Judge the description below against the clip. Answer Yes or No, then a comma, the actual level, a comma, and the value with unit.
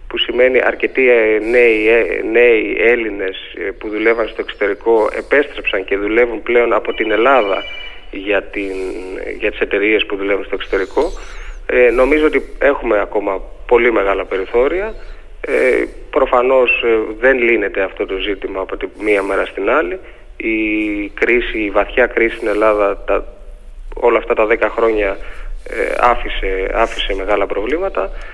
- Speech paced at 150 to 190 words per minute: No, average, 140 wpm